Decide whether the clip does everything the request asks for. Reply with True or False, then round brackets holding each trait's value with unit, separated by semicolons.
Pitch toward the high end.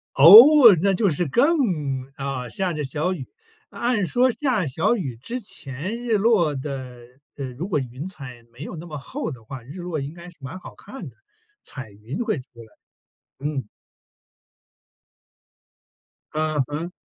False (155 Hz)